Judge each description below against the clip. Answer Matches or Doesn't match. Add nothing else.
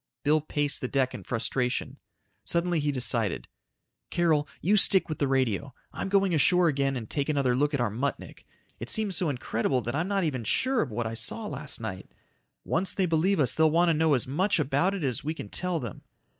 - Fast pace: Matches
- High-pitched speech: Doesn't match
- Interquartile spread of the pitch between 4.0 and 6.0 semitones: Matches